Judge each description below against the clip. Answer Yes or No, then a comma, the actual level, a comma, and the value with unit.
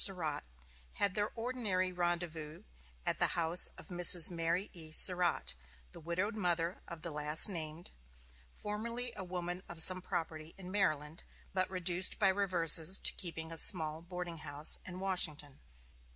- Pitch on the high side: No, medium, 175 Hz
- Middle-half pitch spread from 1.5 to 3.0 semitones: Yes, narrow, 2.5 semitones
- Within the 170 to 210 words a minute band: No, average, 150 wpm